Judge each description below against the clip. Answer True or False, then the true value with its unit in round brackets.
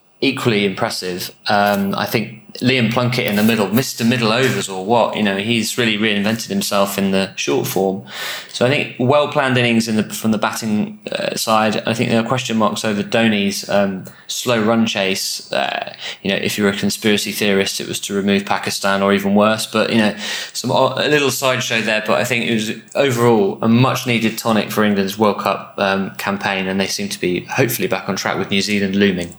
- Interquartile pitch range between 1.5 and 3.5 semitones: True (2.9 semitones)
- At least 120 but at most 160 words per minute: False (205 wpm)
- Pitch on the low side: True (110 Hz)